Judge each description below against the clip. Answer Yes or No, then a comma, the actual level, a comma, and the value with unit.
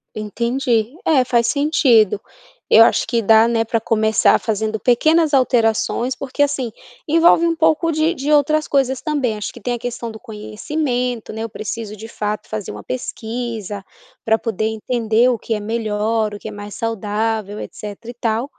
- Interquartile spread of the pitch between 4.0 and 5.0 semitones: No, average, 3.0 semitones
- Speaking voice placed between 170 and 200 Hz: No, high, 230 Hz